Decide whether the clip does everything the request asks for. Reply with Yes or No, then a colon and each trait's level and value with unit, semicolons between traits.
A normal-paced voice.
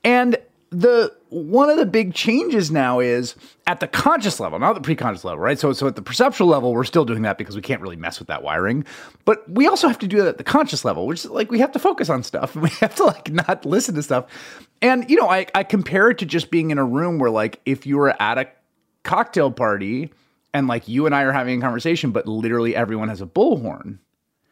No: fast, 245 wpm